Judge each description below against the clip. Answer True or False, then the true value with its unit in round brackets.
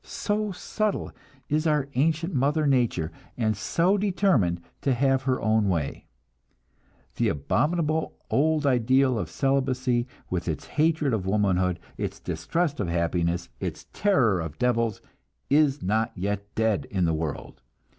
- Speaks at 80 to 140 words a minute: True (135 wpm)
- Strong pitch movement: True (8.2 semitones)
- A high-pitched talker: False (125 Hz)